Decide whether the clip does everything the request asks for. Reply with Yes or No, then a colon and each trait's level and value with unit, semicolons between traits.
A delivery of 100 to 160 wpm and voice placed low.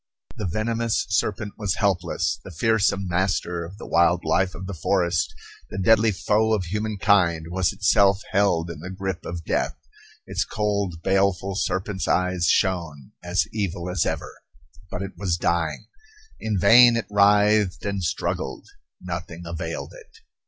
Yes: average, 150 wpm; very low, 95 Hz